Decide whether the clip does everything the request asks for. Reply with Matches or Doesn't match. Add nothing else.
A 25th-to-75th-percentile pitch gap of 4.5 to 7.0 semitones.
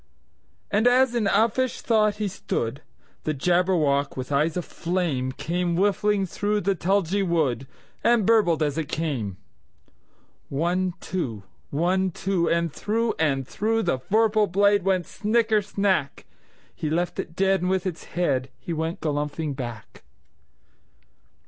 Matches